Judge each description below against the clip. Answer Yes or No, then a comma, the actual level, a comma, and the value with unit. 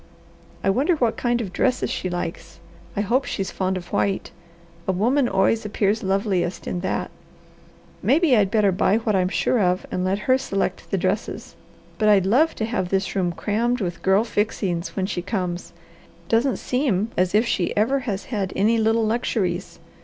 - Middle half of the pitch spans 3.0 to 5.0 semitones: Yes, average, 3.6 semitones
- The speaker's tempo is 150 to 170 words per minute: No, average, 180 wpm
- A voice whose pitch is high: Yes, high, 205 Hz